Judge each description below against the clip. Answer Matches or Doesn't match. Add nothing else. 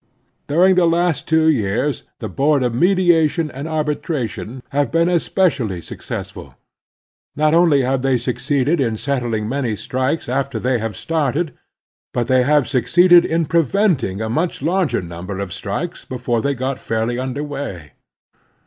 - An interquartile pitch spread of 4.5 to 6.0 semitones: Matches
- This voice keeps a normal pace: Matches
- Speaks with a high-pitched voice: Doesn't match